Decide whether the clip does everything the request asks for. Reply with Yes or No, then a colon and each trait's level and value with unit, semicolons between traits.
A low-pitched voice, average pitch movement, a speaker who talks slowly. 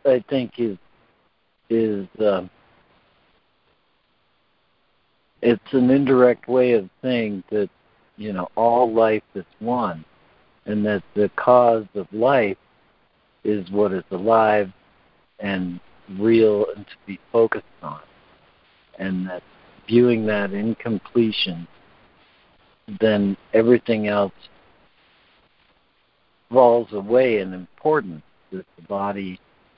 Yes: low, 105 Hz; average, 3.4 semitones; slow, 105 wpm